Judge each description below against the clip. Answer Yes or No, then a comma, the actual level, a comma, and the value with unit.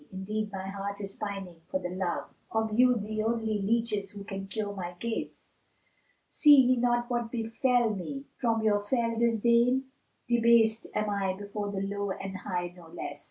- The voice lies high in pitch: Yes, high, 215 Hz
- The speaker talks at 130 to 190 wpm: Yes, average, 180 wpm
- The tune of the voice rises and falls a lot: No, average, 3.1 semitones